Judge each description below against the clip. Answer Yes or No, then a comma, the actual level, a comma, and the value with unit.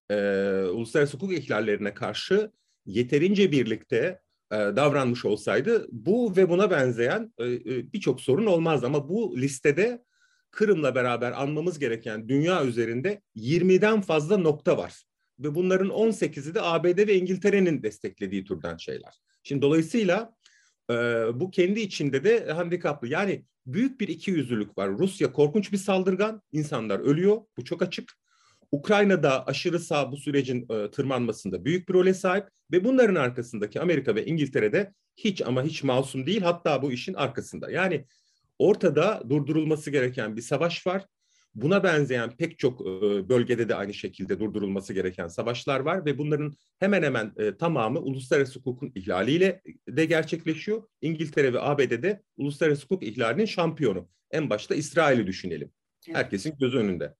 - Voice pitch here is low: No, medium, 155 Hz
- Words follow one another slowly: No, fast, 140 wpm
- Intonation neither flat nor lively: No, wide, 7.5 semitones